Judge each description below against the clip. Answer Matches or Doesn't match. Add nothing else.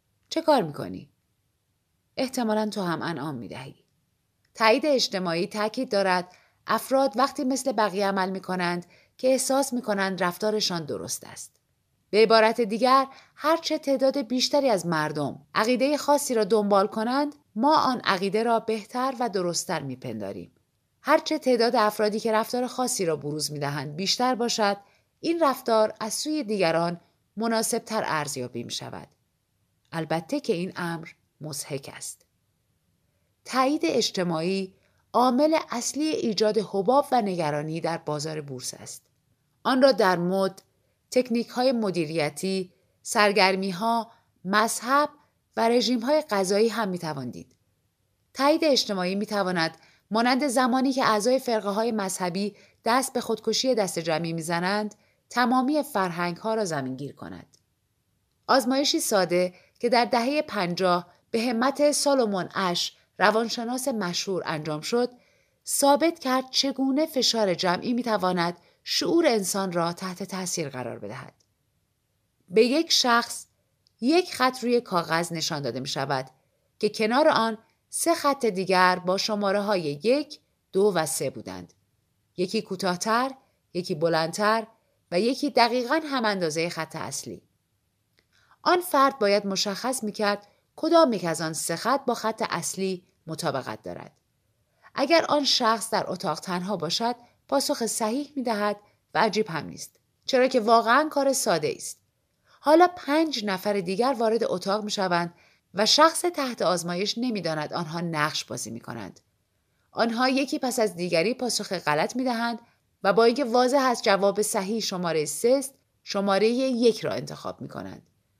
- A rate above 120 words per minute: Matches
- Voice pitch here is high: Matches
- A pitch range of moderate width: Doesn't match